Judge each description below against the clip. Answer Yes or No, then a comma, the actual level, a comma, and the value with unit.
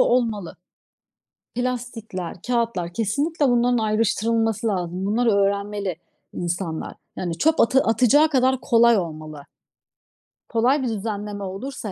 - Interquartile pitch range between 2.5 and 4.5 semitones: Yes, average, 4.0 semitones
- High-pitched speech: Yes, high, 225 Hz